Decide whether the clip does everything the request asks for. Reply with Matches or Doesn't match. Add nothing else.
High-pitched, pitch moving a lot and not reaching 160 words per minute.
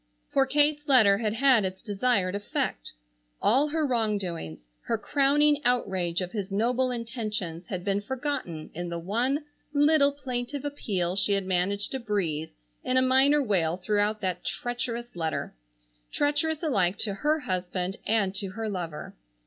Matches